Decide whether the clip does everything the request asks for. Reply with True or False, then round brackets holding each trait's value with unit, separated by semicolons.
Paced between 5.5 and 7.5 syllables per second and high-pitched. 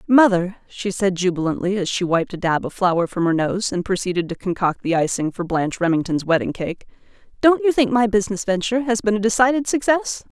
True (5.8 syllables/s; 200 Hz)